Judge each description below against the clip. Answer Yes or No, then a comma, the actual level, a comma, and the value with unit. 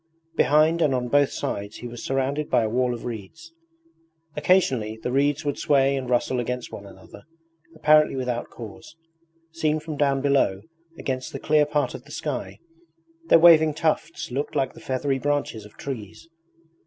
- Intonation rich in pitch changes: No, average, 3.6 semitones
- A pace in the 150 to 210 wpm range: Yes, average, 165 wpm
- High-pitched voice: No, low, 135 Hz